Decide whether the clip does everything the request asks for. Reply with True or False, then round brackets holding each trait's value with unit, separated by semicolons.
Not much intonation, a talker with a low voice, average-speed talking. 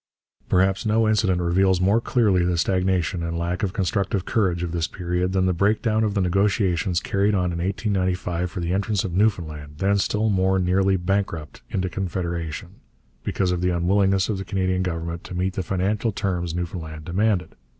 True (2.2 semitones; 95 Hz; 180 wpm)